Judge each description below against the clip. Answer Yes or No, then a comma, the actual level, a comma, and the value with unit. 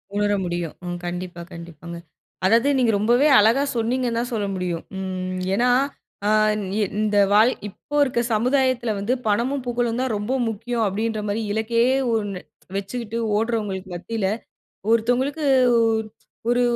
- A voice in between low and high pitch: No, high, 220 Hz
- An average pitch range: Yes, average, 3.7 semitones